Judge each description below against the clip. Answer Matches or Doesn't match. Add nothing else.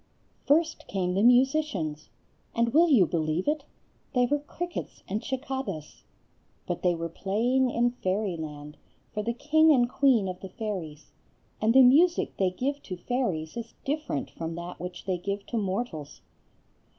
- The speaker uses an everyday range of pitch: Doesn't match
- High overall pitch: Matches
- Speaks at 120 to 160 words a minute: Matches